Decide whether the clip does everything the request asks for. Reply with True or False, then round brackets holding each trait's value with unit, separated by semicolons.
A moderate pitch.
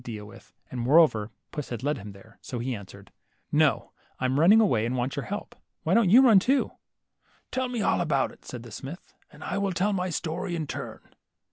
True (145 Hz)